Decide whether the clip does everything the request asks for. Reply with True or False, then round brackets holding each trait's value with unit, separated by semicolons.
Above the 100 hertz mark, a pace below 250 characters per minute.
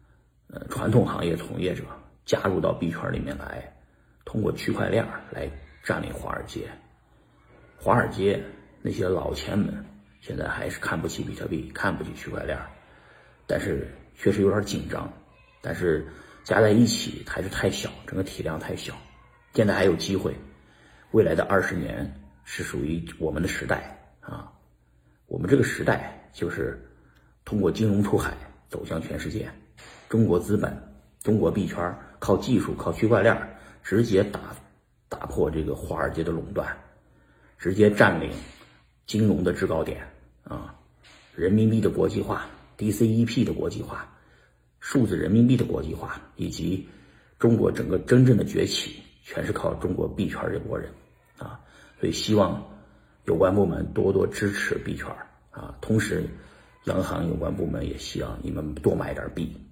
False (80 Hz; 235 characters per minute)